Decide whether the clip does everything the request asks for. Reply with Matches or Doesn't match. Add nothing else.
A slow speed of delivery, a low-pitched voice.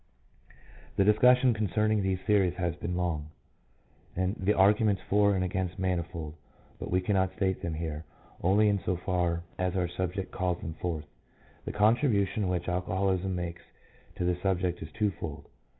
Doesn't match